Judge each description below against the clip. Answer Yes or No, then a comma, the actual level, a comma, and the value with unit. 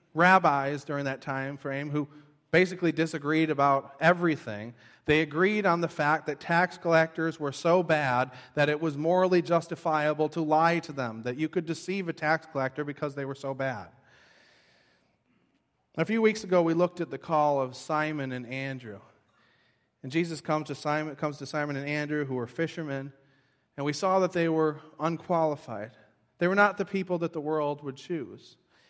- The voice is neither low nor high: Yes, medium, 150 Hz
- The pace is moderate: Yes, average, 175 wpm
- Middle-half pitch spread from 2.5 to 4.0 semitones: Yes, average, 3.5 semitones